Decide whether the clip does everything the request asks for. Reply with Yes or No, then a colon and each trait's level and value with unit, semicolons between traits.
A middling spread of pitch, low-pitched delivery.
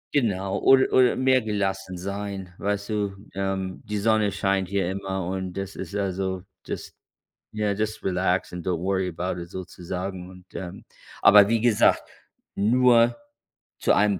No: narrow, 2.1 semitones; very low, 95 Hz